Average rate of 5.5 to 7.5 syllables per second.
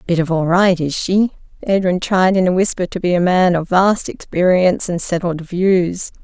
No: 4.8 syllables/s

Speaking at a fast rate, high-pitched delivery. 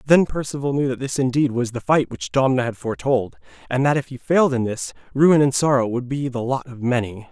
No: fast, 240 wpm; low, 130 Hz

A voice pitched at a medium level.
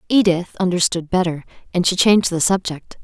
Yes: medium, 180 Hz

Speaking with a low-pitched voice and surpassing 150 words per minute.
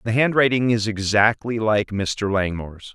No: low, 110 Hz; average, 140 wpm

